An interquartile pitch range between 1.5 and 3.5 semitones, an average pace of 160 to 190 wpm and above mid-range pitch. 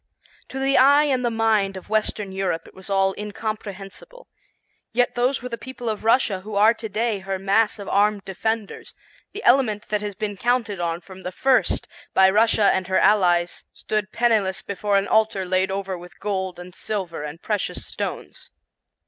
Yes: average, 2.9 semitones; average, 180 wpm; high, 205 Hz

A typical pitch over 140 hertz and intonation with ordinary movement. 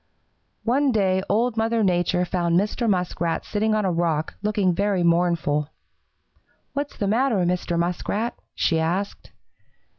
Yes: high, 190 Hz; average, 3.9 semitones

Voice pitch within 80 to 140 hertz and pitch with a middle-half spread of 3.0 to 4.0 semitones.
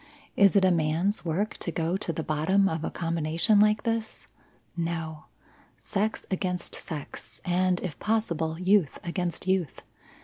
No: medium, 180 Hz; average, 3.5 semitones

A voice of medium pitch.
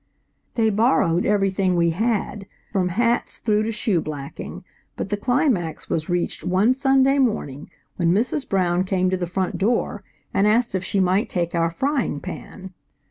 No: high, 195 Hz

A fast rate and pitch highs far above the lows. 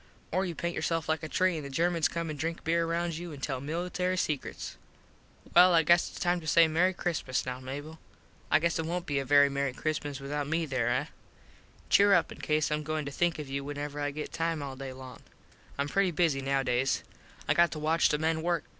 No: fast, 225 wpm; average, 3.1 semitones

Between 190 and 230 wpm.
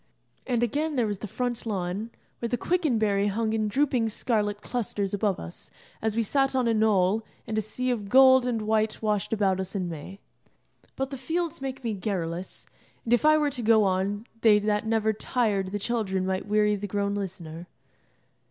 Yes: average, 195 wpm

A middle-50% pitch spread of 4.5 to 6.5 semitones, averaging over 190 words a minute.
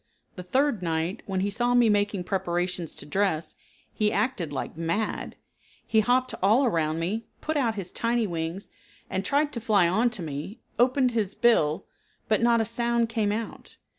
No: average, 5.0 semitones; average, 170 wpm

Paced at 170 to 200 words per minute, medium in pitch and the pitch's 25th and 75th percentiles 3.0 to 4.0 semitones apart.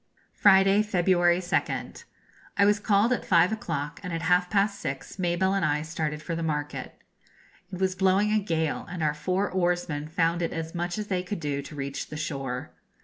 Yes: average, 195 wpm; medium, 175 Hz; average, 3.6 semitones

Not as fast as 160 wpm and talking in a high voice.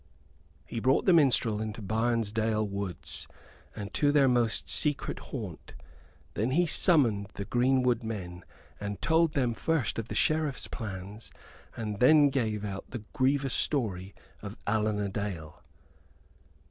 No: slow, 135 wpm; low, 115 Hz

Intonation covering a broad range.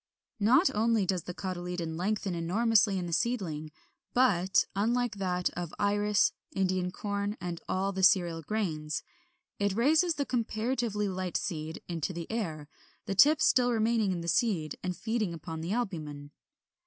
No: average, 4.3 semitones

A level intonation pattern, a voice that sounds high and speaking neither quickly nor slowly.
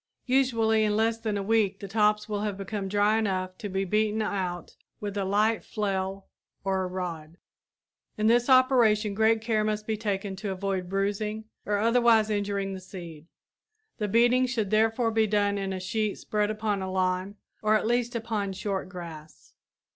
Yes: narrow, 2.3 semitones; high, 210 Hz; average, 175 wpm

